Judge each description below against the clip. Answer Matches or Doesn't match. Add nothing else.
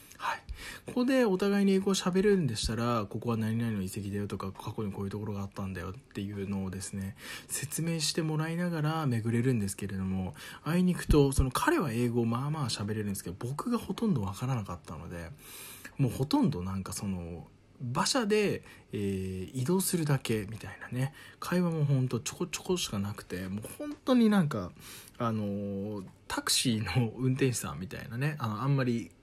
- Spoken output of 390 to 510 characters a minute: Matches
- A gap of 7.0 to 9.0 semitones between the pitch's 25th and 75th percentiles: Matches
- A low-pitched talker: Matches